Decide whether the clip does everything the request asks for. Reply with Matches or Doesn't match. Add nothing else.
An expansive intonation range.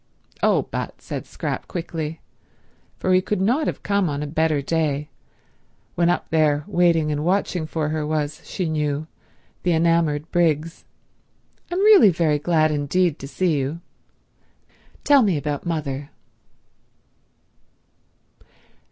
Doesn't match